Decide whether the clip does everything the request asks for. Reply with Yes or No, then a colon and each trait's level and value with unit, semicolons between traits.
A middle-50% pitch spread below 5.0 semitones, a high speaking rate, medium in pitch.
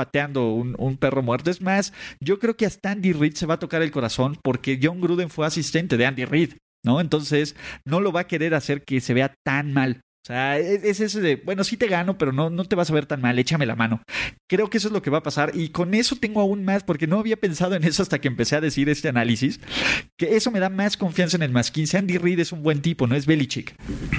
No: wide, 5.4 semitones; fast, 270 wpm; medium, 160 Hz